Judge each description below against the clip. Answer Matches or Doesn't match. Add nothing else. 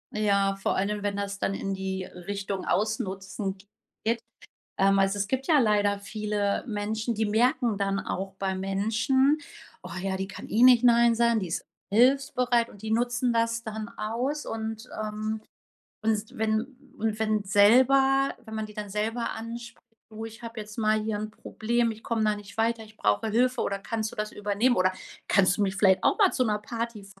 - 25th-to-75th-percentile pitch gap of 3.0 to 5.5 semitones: Doesn't match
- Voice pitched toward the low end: Doesn't match